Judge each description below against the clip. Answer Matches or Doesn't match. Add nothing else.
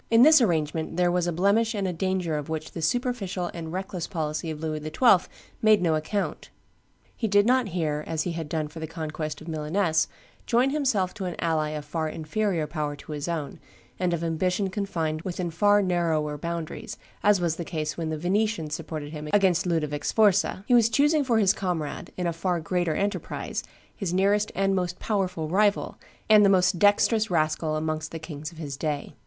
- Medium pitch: Matches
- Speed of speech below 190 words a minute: Doesn't match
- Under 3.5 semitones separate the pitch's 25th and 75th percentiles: Doesn't match